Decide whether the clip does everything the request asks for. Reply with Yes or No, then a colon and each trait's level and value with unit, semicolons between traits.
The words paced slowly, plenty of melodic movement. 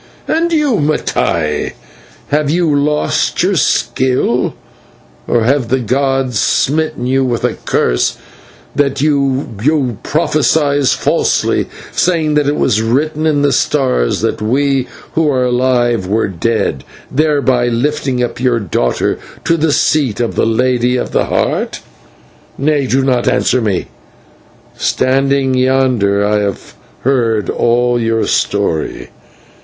No: slow, 130 wpm; average, 3.8 semitones